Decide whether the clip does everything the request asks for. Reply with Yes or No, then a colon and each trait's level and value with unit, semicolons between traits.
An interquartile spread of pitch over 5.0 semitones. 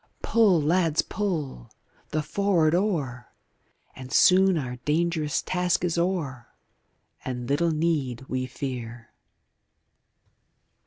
Yes: wide, 5.4 semitones